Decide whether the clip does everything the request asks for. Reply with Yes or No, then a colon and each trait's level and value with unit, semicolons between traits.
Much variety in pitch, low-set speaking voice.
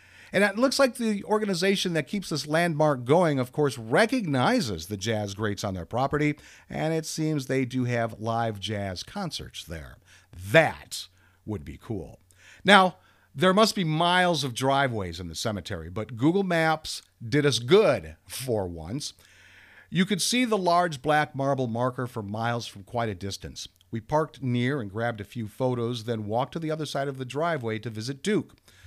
Yes: wide, 7.1 semitones; low, 130 Hz